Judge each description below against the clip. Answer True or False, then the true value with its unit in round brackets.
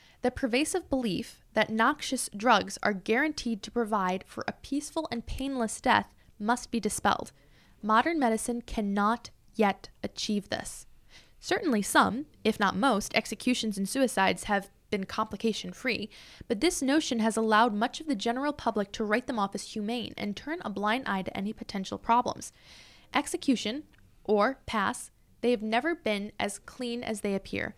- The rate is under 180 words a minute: True (160 wpm)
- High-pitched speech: True (230 Hz)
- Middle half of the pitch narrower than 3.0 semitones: False (3.6 semitones)